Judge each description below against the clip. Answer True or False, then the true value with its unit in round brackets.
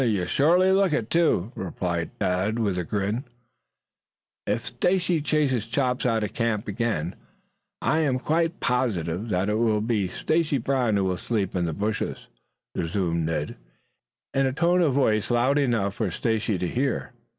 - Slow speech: False (160 wpm)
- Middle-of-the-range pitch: False (115 Hz)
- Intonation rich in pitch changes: True (6.0 semitones)